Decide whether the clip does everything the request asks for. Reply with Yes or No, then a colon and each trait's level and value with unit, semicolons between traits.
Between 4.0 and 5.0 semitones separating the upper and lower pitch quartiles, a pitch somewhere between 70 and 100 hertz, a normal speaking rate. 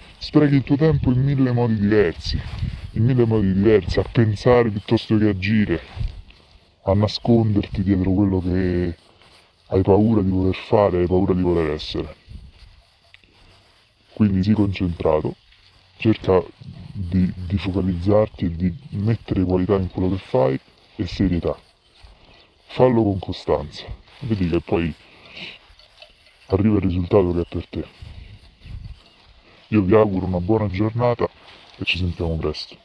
No: average, 3.2 semitones; very low, 95 Hz; average, 130 wpm